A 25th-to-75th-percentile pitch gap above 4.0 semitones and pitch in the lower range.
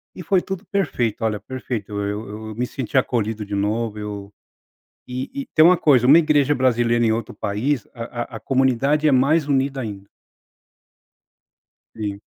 Yes: average, 4.7 semitones; low, 120 Hz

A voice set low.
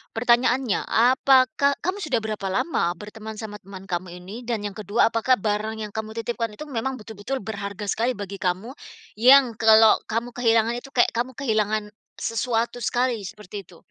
No: high, 225 Hz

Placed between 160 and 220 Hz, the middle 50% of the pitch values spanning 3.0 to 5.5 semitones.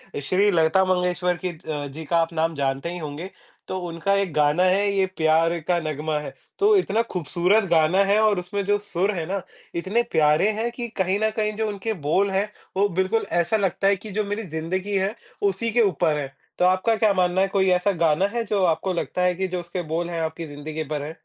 Yes: medium, 185 Hz; average, 3.7 semitones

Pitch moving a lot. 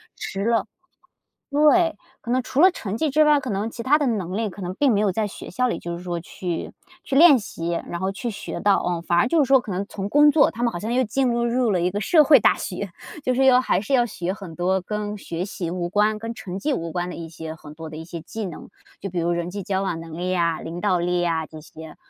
Yes: wide, 6.0 semitones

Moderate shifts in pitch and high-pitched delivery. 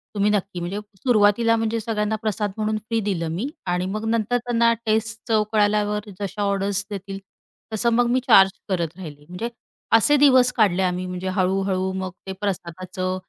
Yes: average, 3.1 semitones; high, 205 Hz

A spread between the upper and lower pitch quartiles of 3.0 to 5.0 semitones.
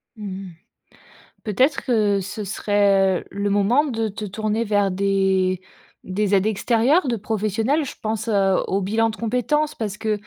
No: narrow, 2.5 semitones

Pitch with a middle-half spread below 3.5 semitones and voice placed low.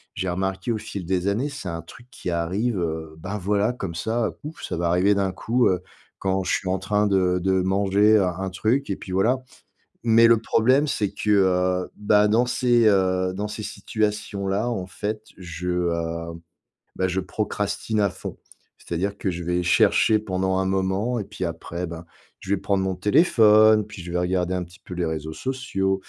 Yes: average, 3.0 semitones; very low, 95 Hz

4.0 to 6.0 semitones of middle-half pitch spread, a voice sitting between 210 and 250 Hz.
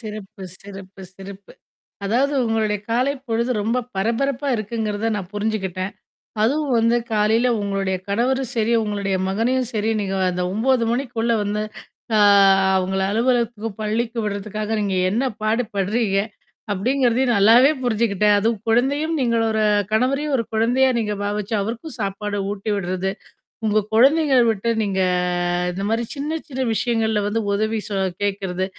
No: average, 3.2 semitones; high, 220 Hz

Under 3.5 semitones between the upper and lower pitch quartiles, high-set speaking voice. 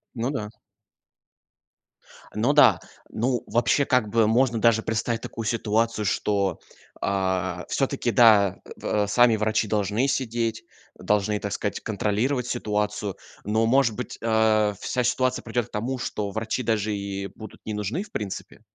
No: narrow, 2.5 semitones; low, 110 Hz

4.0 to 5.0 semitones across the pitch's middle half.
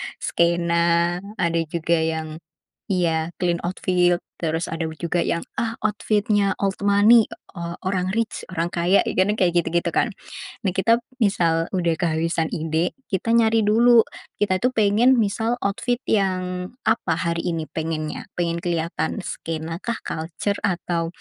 No: average, 3.4 semitones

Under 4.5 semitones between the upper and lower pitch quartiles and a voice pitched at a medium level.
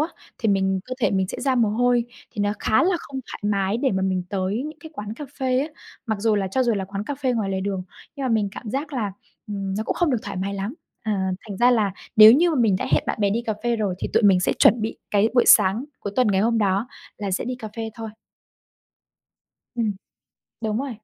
No: average, 3.8 semitones; high, 215 Hz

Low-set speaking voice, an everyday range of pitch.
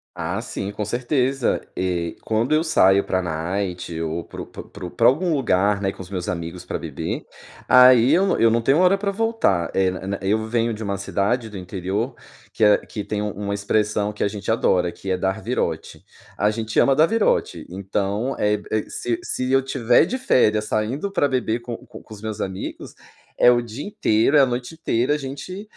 Yes: low, 110 Hz; average, 4.8 semitones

